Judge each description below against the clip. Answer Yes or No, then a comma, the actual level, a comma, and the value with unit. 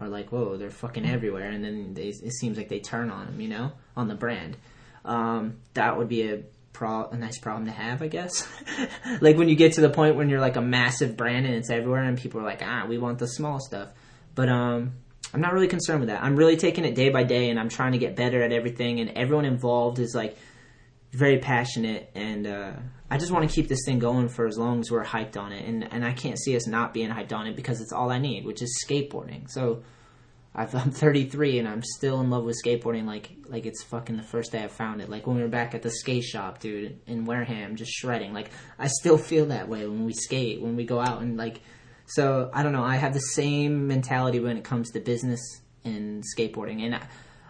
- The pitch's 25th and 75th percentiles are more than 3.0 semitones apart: No, narrow, 2.5 semitones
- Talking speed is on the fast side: Yes, fast, 245 wpm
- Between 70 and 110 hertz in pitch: No, low, 120 Hz